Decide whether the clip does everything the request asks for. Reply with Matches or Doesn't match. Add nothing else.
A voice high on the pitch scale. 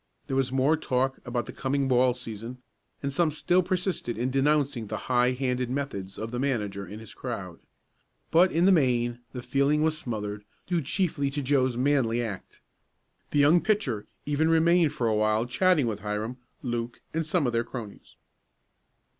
Doesn't match